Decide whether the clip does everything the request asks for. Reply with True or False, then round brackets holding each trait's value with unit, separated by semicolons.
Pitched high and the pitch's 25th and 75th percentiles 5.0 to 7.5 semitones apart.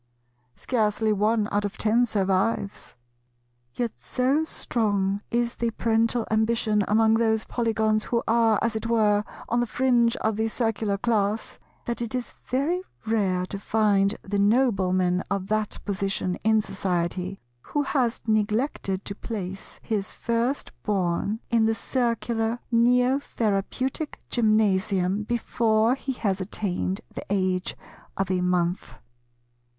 False (220 Hz; 2.8 semitones)